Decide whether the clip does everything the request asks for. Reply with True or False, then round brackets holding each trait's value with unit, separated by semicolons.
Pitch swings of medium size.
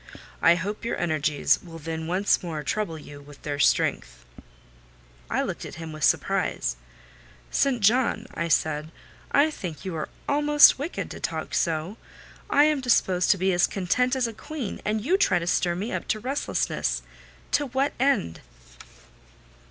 False (8.0 semitones)